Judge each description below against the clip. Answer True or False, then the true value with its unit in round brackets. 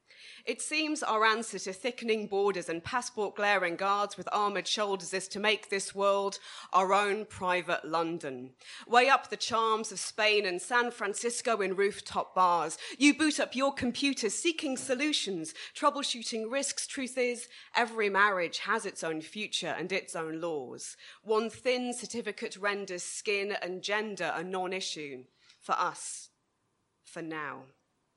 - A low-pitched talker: False (205 Hz)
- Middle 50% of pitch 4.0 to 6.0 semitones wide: True (4.3 semitones)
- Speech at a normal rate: True (150 wpm)